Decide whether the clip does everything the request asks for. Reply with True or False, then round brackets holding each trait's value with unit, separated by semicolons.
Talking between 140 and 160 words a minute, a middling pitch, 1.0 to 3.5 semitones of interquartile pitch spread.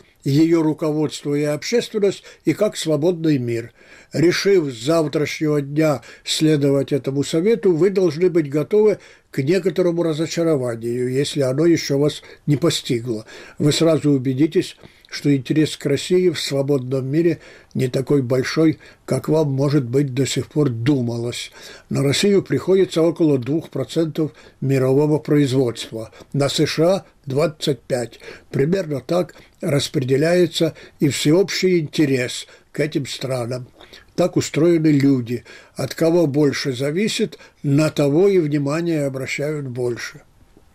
False (120 wpm; 150 Hz; 3.2 semitones)